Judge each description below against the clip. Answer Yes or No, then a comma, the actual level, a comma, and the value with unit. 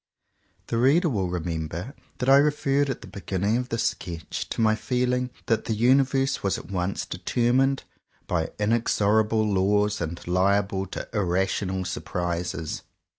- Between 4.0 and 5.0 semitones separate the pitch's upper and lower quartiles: No, wide, 5.4 semitones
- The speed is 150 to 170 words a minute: No, average, 140 wpm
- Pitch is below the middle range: Yes, low, 105 Hz